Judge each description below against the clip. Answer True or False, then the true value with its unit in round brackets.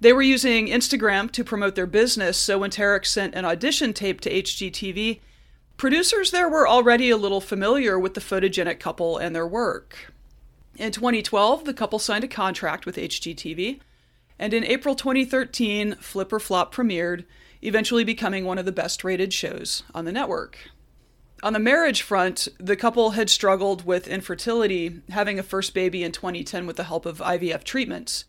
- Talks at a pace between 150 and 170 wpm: True (165 wpm)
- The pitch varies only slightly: False (4.1 semitones)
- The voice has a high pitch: True (200 Hz)